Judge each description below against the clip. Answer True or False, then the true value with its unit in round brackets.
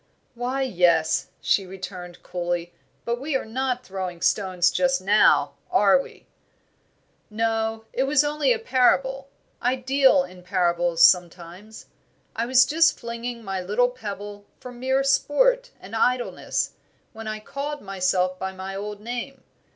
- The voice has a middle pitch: False (225 Hz)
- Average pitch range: False (5.8 semitones)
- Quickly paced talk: False (140 wpm)